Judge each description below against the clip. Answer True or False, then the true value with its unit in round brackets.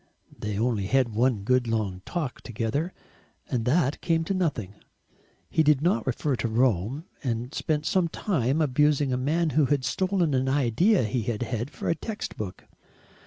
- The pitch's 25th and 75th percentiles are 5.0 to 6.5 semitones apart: True (5.3 semitones)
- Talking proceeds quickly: False (170 wpm)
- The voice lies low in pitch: True (130 Hz)